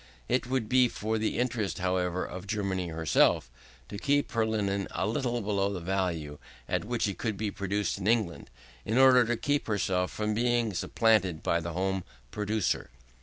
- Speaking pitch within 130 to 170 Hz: No, low, 105 Hz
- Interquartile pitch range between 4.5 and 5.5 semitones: No, average, 3.7 semitones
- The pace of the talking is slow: No, average, 175 wpm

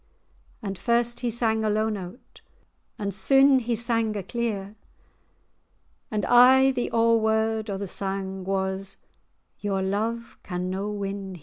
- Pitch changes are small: No, average, 3.2 semitones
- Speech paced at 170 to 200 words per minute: No, average, 140 wpm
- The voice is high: Yes, high, 215 Hz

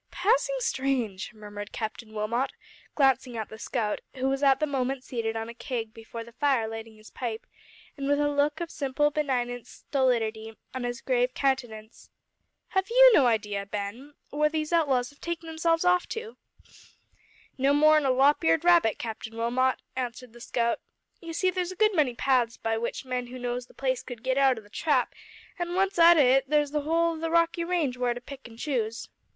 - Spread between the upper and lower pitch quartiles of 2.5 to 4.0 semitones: No, average, 4.7 semitones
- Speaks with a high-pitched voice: Yes, very high, 260 Hz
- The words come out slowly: No, average, 200 wpm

